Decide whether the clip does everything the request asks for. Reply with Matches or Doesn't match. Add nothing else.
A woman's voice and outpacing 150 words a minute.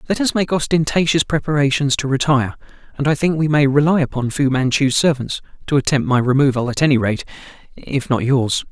Doesn't match